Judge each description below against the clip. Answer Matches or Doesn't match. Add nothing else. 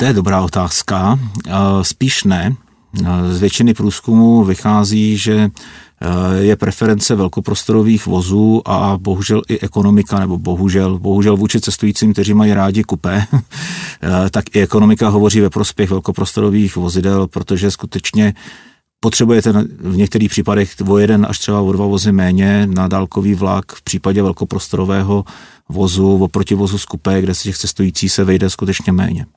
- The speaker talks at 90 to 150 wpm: Matches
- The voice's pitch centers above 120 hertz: Doesn't match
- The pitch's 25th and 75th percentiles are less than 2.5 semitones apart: Matches